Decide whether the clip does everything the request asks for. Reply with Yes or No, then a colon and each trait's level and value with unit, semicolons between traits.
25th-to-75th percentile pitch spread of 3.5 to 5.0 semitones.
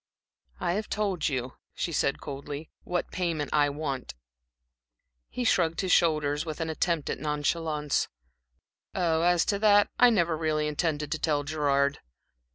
No: average, 2.8 semitones